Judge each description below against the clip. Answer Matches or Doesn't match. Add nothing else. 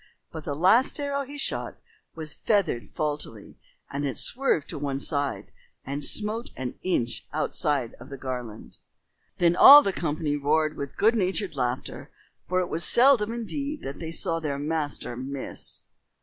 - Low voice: Doesn't match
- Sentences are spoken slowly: Doesn't match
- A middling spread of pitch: Doesn't match